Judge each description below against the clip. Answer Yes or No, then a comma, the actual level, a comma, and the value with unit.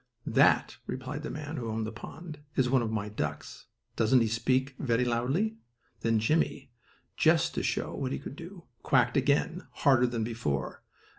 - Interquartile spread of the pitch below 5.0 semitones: Yes, average, 4.2 semitones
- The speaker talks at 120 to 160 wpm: No, average, 170 wpm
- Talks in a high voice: No, low, 125 Hz